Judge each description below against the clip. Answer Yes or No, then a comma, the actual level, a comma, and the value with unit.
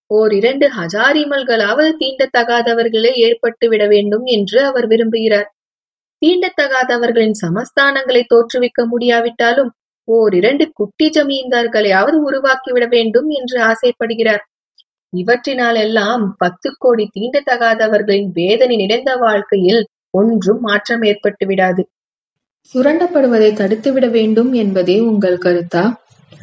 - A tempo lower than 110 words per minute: Yes, average, 85 wpm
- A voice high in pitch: Yes, high, 230 Hz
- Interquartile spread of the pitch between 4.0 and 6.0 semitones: No, average, 3.6 semitones